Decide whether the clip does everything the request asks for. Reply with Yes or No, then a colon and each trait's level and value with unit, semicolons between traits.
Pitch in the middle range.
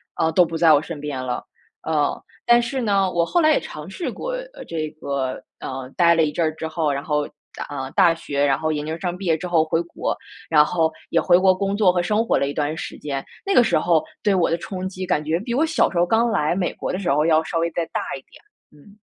Yes: medium, 165 Hz